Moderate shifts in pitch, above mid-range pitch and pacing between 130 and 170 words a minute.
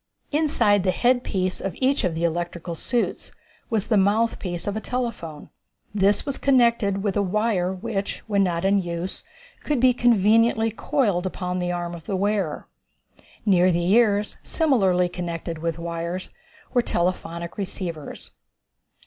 Yes: average, 4.4 semitones; high, 195 Hz; average, 145 wpm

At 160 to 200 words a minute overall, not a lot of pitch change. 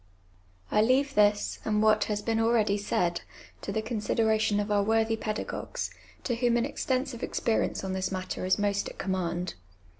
Yes: average, 170 wpm; narrow, 2.0 semitones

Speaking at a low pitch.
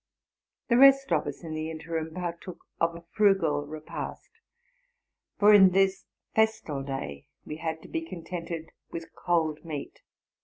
No: medium, 165 Hz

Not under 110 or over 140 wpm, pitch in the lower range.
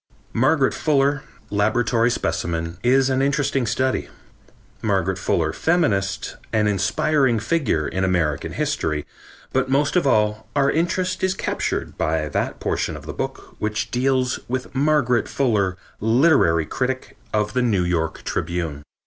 Yes: slow, 135 wpm; low, 115 Hz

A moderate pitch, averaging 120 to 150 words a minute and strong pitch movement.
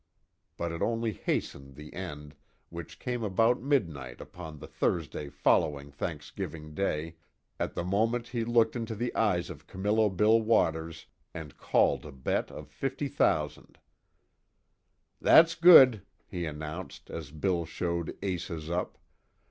No: very low, 85 Hz; slow, 135 wpm; wide, 6.4 semitones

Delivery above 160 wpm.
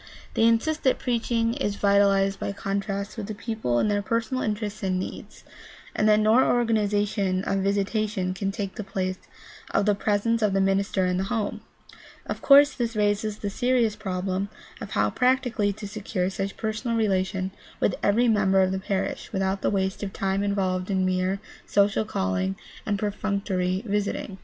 Yes: average, 175 wpm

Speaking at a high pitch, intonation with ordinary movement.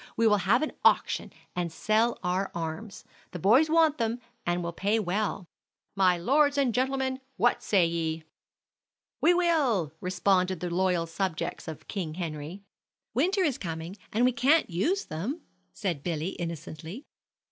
No: high, 195 Hz; wide, 6.7 semitones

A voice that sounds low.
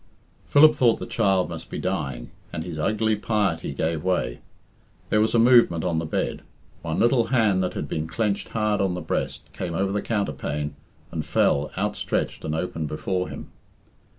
Yes: very low, 95 Hz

